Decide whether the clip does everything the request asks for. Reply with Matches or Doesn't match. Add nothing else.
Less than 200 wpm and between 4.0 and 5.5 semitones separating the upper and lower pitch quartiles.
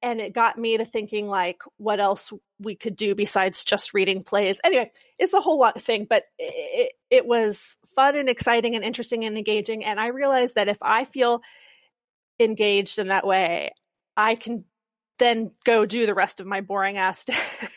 Doesn't match